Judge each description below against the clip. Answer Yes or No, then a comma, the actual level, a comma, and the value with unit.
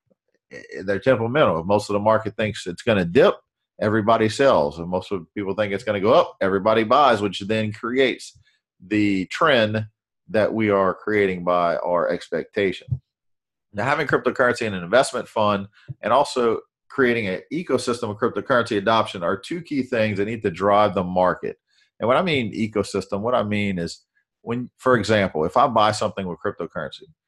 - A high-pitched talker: No, low, 105 Hz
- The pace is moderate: Yes, average, 180 wpm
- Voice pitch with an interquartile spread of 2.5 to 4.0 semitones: Yes, average, 2.9 semitones